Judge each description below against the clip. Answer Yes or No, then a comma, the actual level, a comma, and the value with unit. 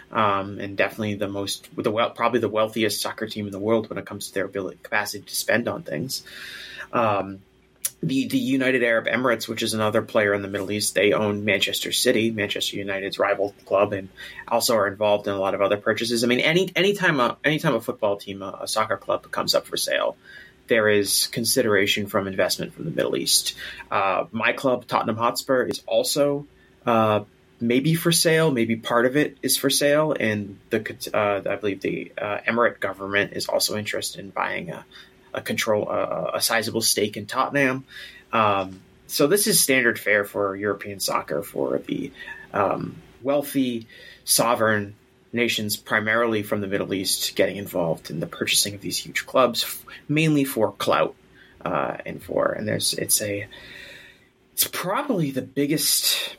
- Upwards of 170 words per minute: Yes, average, 180 wpm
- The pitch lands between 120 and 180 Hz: No, low, 110 Hz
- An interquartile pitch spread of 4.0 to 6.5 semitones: Yes, average, 4.3 semitones